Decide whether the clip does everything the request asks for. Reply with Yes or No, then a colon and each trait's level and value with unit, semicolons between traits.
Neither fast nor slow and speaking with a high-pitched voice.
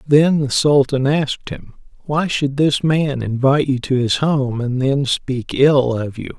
No: average, 190 wpm; low, 135 Hz